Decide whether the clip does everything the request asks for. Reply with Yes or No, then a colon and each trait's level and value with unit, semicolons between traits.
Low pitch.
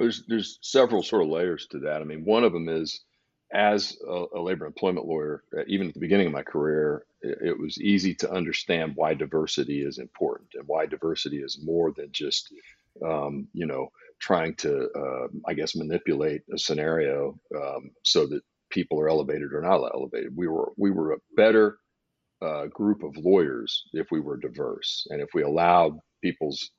Yes: low, 110 Hz